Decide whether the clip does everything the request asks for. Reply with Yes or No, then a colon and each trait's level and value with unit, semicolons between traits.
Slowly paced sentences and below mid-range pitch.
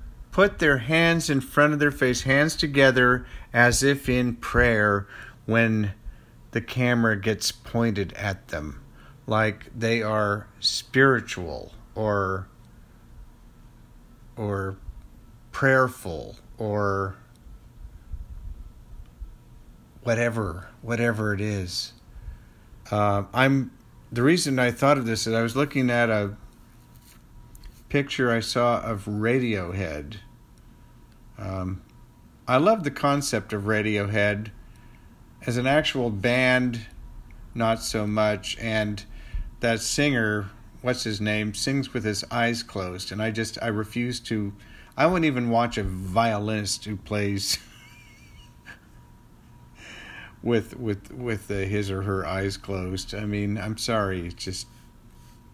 Yes: slow, 115 wpm; low, 110 Hz